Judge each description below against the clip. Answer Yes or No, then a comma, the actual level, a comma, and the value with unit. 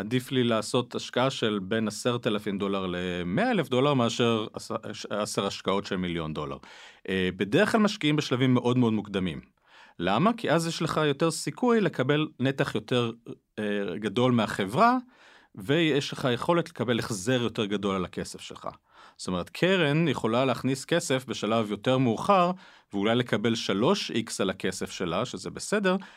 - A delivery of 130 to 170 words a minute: Yes, average, 145 wpm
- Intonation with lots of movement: Yes, wide, 6.1 semitones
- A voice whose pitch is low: Yes, low, 125 Hz